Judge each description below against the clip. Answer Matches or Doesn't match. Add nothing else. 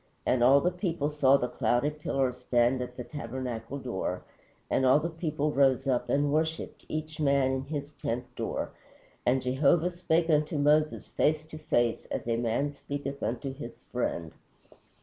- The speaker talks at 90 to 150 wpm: Doesn't match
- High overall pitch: Doesn't match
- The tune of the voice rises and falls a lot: Doesn't match